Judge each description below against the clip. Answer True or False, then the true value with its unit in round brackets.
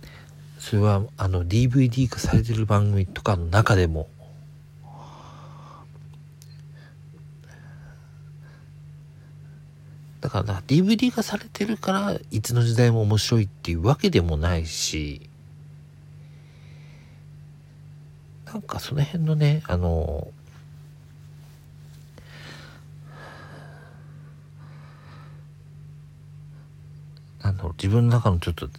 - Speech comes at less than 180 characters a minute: True (165 characters per minute)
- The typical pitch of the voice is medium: True (145 Hz)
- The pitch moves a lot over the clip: False (4.2 semitones)